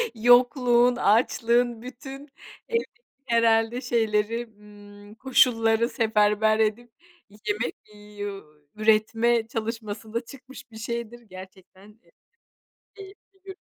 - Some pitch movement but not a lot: No, narrow, 2.2 semitones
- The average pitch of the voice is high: Yes, high, 230 Hz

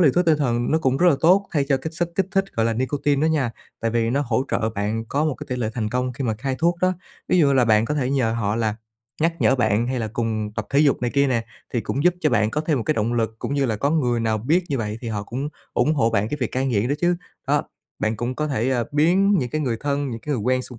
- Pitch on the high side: No, low, 130 Hz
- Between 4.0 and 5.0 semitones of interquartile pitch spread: Yes, average, 4.7 semitones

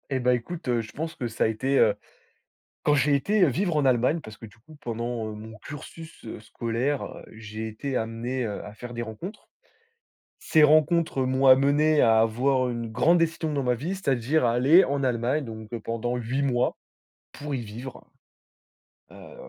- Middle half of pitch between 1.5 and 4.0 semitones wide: No, average, 4.4 semitones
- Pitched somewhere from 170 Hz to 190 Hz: No, low, 130 Hz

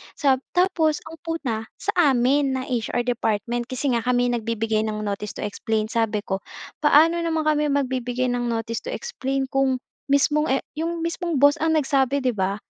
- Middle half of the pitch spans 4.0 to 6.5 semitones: Yes, average, 4.7 semitones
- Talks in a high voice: Yes, very high, 260 Hz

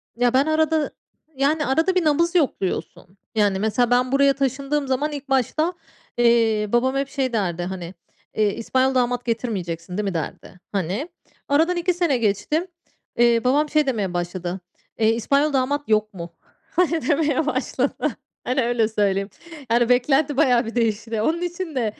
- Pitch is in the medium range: No, very high, 250 Hz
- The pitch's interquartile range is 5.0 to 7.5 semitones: Yes, wide, 5.4 semitones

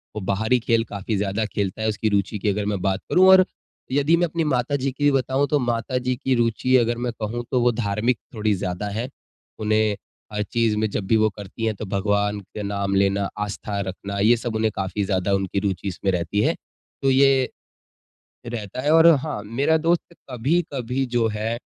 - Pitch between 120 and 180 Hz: No, low, 110 Hz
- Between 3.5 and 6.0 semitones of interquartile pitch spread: Yes, average, 3.9 semitones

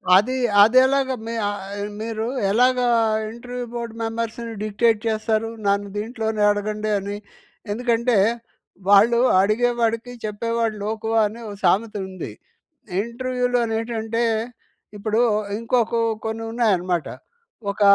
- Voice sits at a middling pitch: No, high, 225 Hz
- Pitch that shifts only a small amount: Yes, narrow, 1.9 semitones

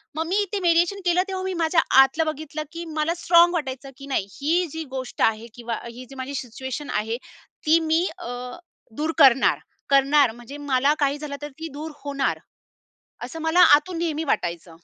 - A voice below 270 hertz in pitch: No, very high, 295 Hz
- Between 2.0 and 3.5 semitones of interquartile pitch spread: No, average, 3.9 semitones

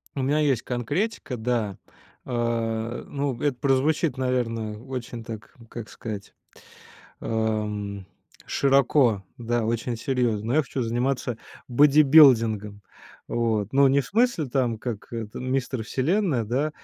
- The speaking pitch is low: Yes, low, 120 Hz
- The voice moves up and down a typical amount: Yes, average, 3.5 semitones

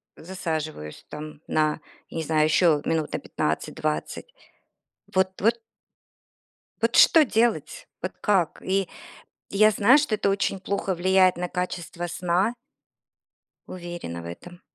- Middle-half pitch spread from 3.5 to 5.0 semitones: Yes, average, 3.8 semitones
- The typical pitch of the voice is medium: Yes, medium, 180 Hz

